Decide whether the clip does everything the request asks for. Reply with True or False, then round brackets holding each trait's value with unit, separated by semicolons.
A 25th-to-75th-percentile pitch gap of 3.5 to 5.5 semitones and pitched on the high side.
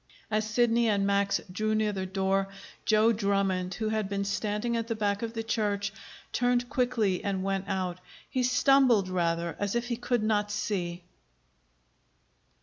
False (2.7 semitones; 210 Hz)